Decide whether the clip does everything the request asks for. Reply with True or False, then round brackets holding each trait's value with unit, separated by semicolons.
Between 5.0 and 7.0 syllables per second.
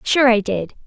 False (4.6 syllables/s)